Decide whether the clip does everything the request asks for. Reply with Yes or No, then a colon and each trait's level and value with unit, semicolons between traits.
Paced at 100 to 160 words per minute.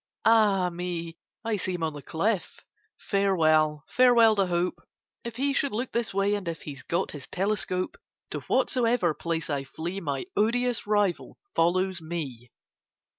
Yes: average, 155 wpm